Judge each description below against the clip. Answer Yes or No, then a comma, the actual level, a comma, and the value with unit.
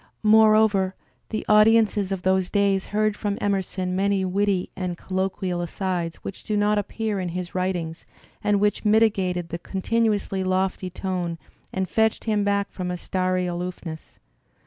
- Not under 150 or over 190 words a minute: Yes, average, 155 wpm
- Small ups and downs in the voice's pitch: Yes, narrow, 2.2 semitones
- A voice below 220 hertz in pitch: Yes, high, 190 Hz